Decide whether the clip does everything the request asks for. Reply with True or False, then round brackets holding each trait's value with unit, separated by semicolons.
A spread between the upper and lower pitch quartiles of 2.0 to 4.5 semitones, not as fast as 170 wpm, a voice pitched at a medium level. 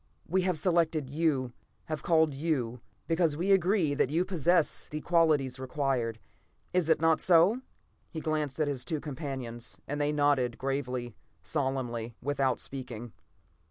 True (4.0 semitones; 150 wpm; 145 Hz)